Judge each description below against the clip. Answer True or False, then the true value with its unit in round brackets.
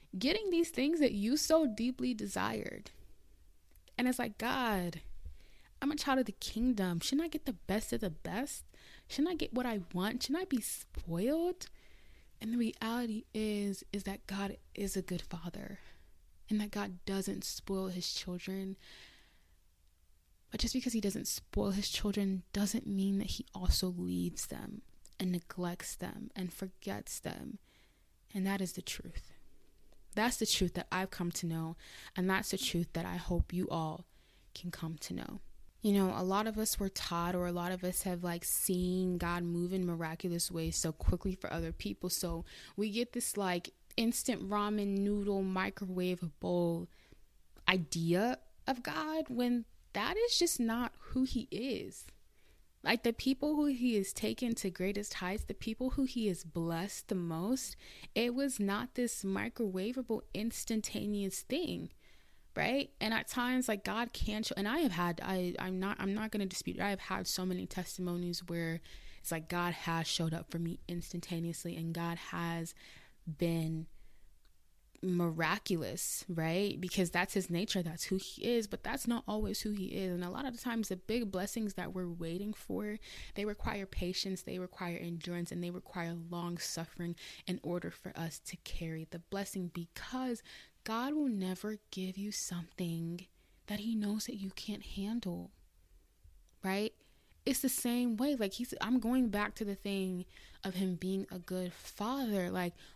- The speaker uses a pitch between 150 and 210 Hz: True (190 Hz)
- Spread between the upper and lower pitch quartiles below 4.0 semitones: False (4.4 semitones)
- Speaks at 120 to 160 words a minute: False (175 wpm)